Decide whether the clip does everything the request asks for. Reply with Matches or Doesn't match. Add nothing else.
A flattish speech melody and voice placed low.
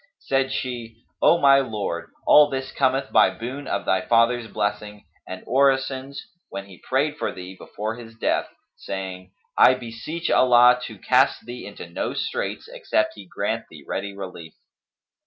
Doesn't match